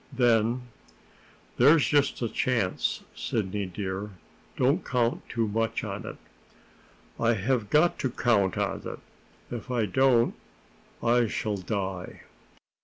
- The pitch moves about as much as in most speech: Yes, average, 3.6 semitones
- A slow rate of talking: Yes, slow, 120 wpm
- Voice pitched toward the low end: Yes, low, 115 Hz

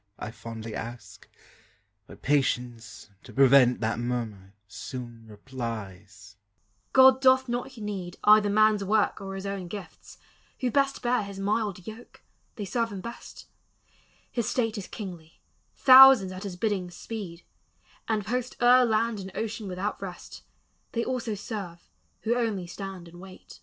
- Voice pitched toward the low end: No, high, 195 Hz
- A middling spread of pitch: No, wide, 8.4 semitones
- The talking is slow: No, average, 145 wpm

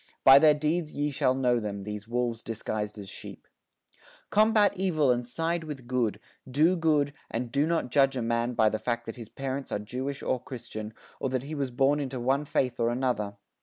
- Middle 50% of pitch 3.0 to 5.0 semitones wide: Yes, average, 3.8 semitones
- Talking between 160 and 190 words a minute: No, fast, 205 wpm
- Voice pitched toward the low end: Yes, low, 130 Hz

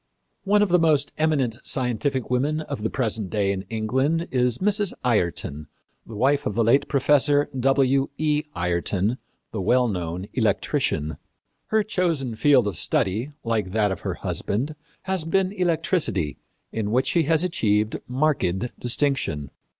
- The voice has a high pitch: No, low, 125 Hz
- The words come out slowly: No, average, 150 wpm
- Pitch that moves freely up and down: Yes, wide, 6.4 semitones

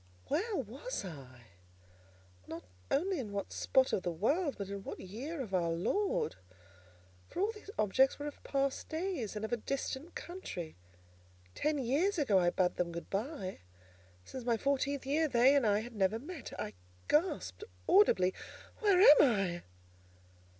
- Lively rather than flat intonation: Yes, wide, 8.2 semitones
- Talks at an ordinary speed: Yes, average, 160 wpm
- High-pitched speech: Yes, very high, 260 Hz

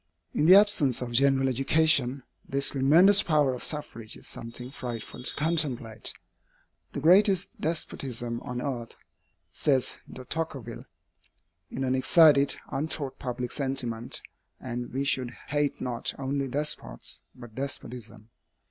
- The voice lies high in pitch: No, low, 135 Hz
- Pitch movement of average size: Yes, average, 3.4 semitones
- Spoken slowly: Yes, slow, 125 wpm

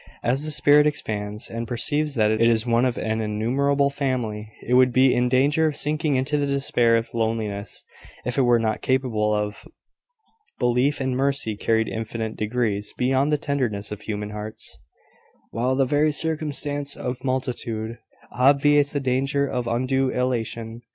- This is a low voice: Yes, low, 125 Hz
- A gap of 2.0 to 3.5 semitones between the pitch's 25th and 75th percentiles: No, average, 3.9 semitones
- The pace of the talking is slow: No, average, 160 wpm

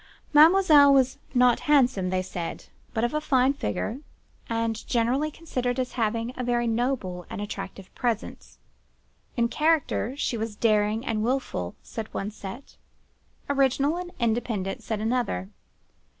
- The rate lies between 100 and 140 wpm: Yes, slow, 135 wpm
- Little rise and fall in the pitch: No, average, 4.1 semitones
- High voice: Yes, high, 240 Hz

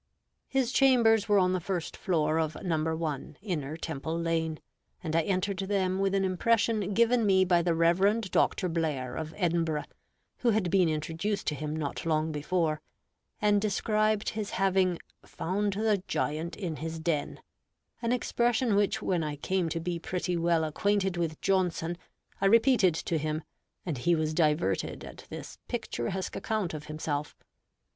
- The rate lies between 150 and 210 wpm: Yes, average, 160 wpm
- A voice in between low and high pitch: Yes, medium, 175 Hz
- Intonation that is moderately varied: Yes, average, 4.1 semitones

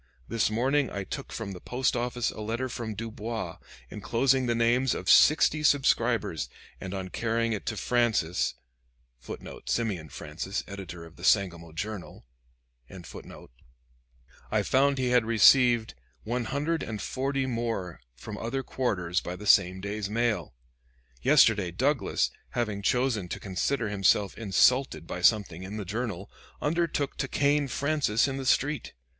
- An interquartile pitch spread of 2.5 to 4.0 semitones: No, average, 4.8 semitones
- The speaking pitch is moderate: No, low, 115 Hz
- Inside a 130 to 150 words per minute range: Yes, average, 140 wpm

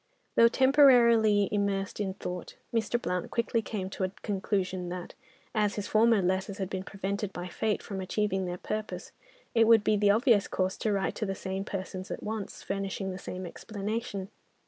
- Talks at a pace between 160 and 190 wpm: Yes, average, 180 wpm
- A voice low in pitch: No, high, 200 Hz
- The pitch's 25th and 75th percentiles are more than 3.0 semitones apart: No, narrow, 2.4 semitones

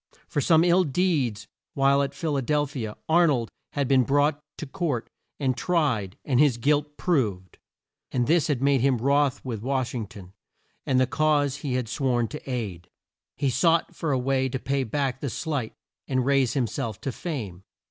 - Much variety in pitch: No, average, 3.3 semitones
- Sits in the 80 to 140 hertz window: Yes, low, 135 Hz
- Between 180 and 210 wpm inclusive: Yes, average, 195 wpm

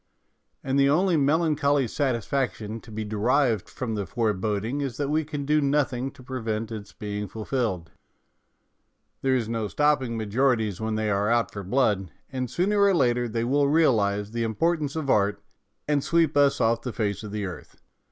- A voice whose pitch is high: No, low, 120 Hz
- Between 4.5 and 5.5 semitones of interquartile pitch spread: Yes, average, 4.8 semitones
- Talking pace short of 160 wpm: No, average, 175 wpm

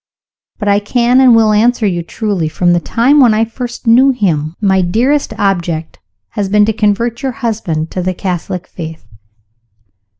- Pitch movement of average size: Yes, average, 4.9 semitones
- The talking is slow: No, average, 170 wpm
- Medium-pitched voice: No, high, 210 Hz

